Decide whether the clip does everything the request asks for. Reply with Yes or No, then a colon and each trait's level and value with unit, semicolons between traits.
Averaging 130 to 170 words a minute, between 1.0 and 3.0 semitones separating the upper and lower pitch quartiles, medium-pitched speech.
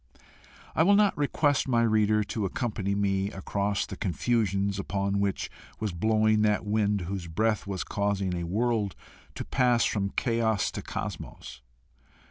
No: average, 145 wpm; narrow, 2.4 semitones; low, 105 Hz